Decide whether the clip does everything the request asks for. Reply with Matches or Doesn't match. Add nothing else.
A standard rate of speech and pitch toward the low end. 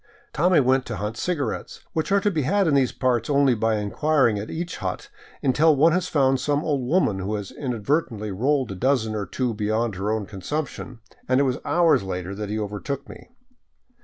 Doesn't match